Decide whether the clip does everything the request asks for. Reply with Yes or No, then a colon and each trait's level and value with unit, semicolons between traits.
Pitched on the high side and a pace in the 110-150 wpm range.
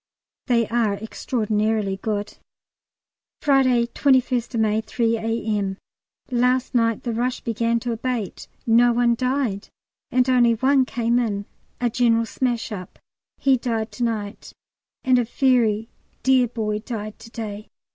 Yes: high, 230 Hz; slow, 135 wpm